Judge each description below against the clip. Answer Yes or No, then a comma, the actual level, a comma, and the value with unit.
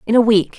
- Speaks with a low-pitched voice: No, high, 220 Hz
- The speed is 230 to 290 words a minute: No, fast, 305 wpm